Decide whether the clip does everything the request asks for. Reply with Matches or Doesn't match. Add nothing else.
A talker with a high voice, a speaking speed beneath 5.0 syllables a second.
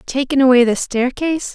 Doesn't match